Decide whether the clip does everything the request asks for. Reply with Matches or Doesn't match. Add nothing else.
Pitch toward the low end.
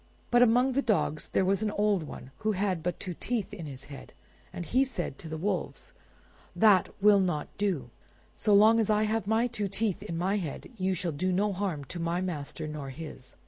Doesn't match